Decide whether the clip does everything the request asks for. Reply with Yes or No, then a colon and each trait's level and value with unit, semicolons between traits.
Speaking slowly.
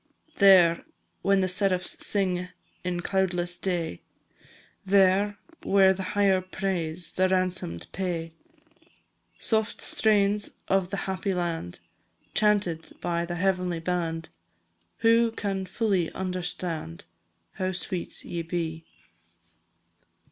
Yes: slow, 105 wpm